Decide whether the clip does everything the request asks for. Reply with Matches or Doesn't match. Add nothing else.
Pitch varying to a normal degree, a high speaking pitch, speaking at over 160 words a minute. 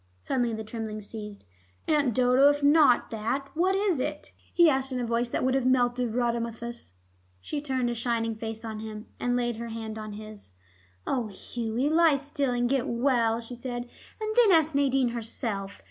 Matches